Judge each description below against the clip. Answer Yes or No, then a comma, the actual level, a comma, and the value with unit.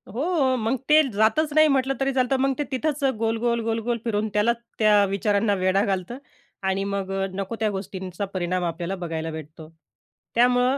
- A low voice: No, high, 215 Hz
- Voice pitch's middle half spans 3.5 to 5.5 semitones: Yes, average, 5.0 semitones